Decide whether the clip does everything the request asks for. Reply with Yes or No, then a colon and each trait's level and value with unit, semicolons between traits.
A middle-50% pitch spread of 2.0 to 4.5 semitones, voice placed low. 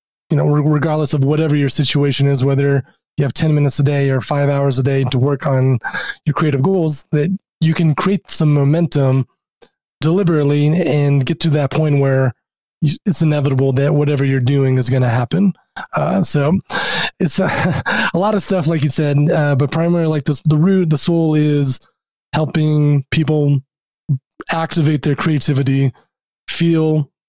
No: narrow, 2.6 semitones; medium, 150 Hz